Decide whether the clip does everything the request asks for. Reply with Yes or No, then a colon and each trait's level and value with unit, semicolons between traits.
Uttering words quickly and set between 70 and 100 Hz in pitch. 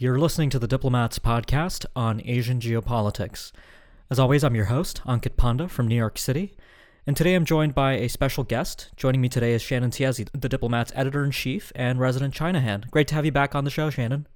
No: fast, 210 wpm; low, 130 Hz